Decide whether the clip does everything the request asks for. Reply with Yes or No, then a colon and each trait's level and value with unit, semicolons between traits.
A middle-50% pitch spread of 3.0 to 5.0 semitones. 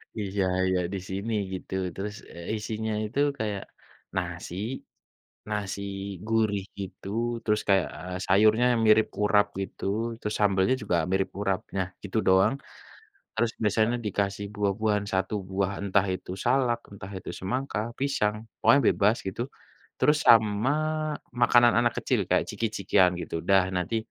No: narrow, 2.4 semitones